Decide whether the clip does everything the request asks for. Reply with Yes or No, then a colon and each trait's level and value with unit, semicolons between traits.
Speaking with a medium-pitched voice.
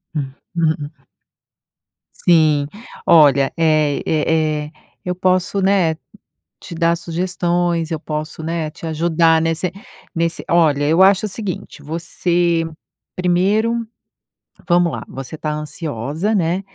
Yes: medium, 165 Hz